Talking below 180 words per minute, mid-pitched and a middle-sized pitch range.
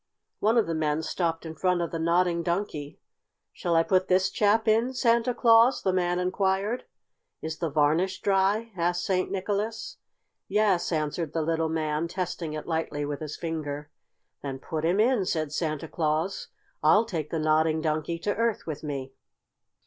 Yes: average, 170 wpm; medium, 170 Hz; average, 3.8 semitones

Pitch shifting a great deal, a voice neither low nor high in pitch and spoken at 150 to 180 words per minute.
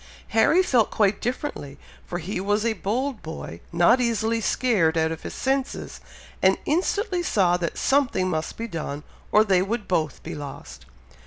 No: wide, 6.6 semitones; high, 205 Hz; average, 165 wpm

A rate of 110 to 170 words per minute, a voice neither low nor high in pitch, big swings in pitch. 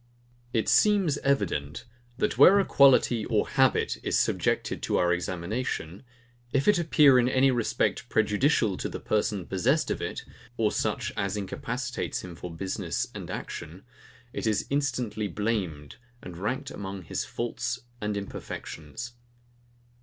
No: average, 140 wpm; low, 110 Hz; wide, 5.7 semitones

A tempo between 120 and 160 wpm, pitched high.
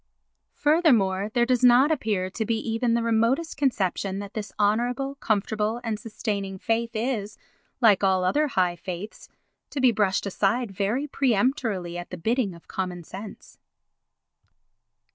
Yes: average, 145 wpm; high, 220 Hz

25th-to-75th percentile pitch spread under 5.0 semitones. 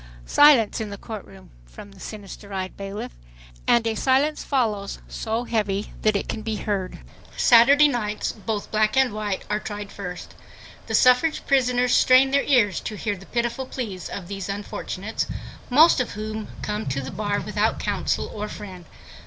Yes: average, 3.5 semitones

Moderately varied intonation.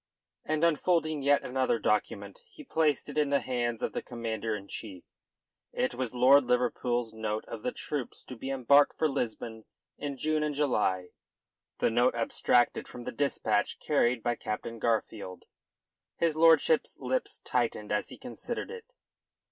Yes: average, 4.4 semitones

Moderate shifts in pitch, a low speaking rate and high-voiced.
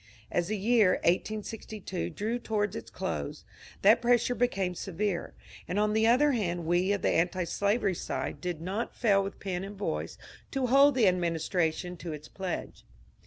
No: average, 3.9 semitones; average, 165 wpm; high, 195 Hz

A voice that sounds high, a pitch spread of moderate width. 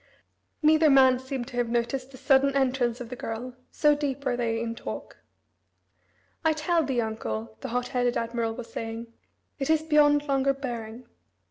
Yes: very high, 255 Hz; average, 3.0 semitones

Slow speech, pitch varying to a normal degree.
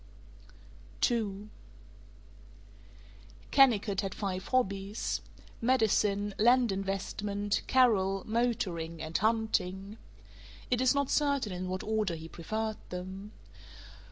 Yes: slow, 95 wpm; average, 3.0 semitones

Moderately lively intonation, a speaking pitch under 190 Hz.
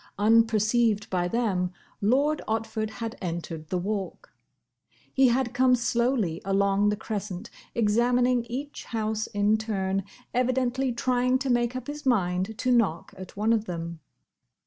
No: average, 3.8 semitones; high, 220 Hz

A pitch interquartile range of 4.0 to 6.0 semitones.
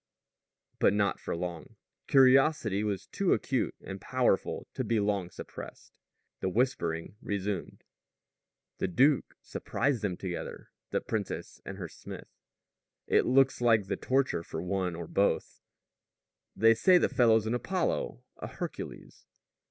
Yes: average, 5.3 semitones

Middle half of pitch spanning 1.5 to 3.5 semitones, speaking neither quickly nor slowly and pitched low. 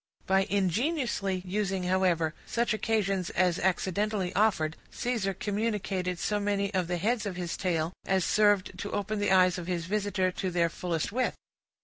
No: narrow, 2.5 semitones; average, 160 wpm; high, 190 Hz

